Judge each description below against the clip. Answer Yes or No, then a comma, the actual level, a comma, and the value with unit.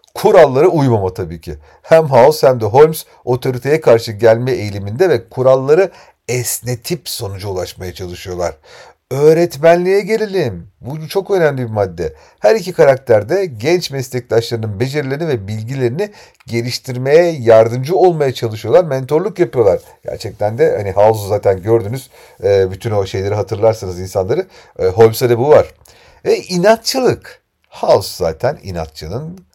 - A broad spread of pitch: Yes, wide, 7.3 semitones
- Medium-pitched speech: No, low, 125 Hz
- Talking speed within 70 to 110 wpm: No, average, 125 wpm